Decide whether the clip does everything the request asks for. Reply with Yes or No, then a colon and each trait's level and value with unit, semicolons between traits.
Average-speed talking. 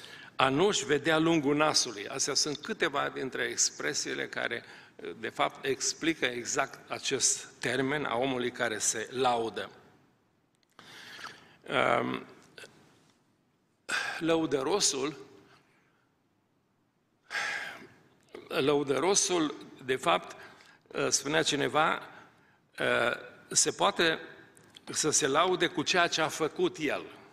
No: slow, 85 wpm